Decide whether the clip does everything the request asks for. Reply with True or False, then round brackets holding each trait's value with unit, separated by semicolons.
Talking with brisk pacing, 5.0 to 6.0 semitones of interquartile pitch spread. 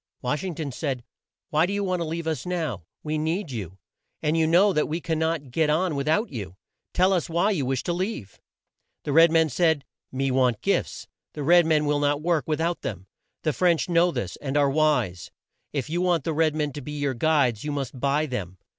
False (225 wpm; 3.6 semitones)